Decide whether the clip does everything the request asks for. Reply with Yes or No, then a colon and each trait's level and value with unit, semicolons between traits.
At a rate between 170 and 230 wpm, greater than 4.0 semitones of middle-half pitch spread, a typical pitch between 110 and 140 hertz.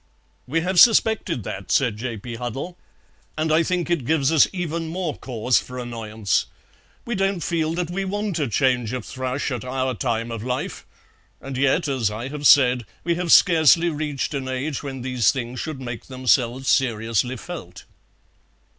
Yes: average, 175 wpm; average, 5.1 semitones; low, 135 Hz